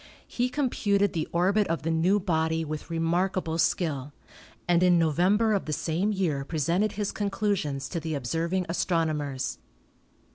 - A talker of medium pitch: Yes, medium, 170 Hz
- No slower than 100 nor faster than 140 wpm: No, average, 150 wpm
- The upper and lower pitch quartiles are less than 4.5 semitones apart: Yes, average, 3.6 semitones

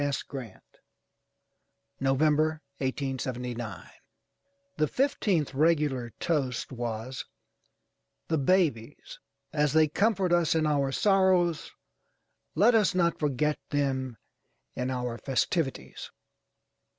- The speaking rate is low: Yes, slow, 90 wpm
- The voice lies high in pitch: No, medium, 145 Hz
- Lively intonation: No, average, 4.5 semitones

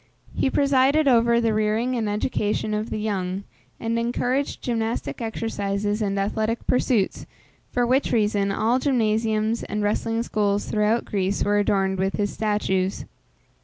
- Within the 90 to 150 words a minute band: Yes, average, 140 wpm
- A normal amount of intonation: No, narrow, 2.3 semitones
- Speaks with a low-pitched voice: No, high, 215 Hz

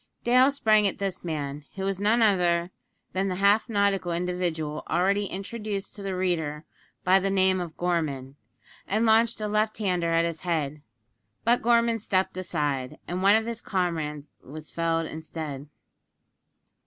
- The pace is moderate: Yes, average, 155 wpm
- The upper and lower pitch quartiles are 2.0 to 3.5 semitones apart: No, average, 3.9 semitones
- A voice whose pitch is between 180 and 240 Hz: Yes, medium, 185 Hz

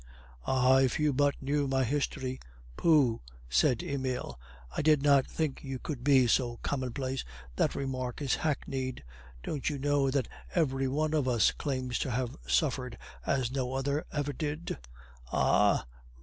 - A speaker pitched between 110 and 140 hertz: Yes, low, 135 Hz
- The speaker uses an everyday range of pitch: No, narrow, 2.1 semitones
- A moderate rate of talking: Yes, average, 150 wpm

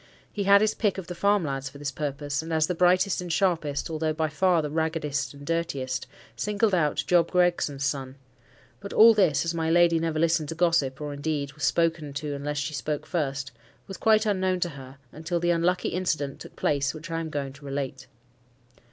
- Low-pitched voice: No, medium, 160 Hz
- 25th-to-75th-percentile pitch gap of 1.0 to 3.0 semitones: No, average, 3.6 semitones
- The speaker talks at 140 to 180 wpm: No, average, 200 wpm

